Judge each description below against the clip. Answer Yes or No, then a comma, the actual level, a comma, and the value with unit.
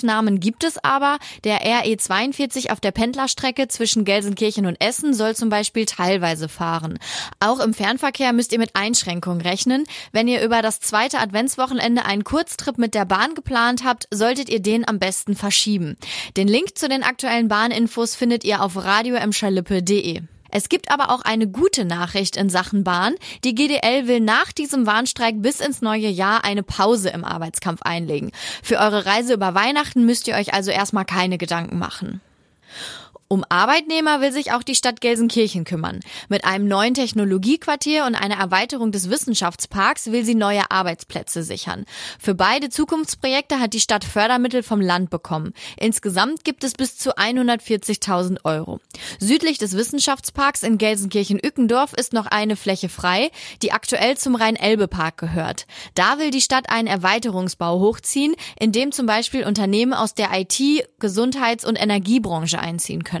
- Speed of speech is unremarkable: Yes, average, 160 wpm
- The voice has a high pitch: Yes, high, 220 Hz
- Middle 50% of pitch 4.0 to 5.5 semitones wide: Yes, average, 4.3 semitones